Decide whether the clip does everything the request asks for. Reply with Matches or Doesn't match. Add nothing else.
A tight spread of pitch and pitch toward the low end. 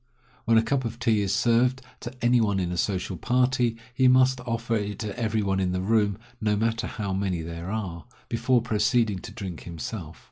Doesn't match